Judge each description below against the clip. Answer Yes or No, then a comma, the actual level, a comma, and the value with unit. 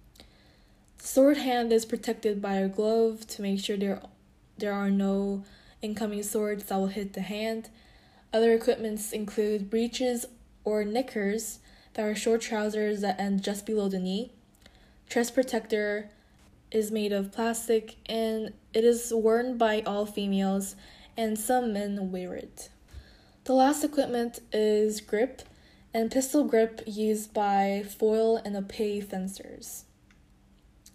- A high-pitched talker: Yes, high, 215 Hz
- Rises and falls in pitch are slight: Yes, narrow, 2.2 semitones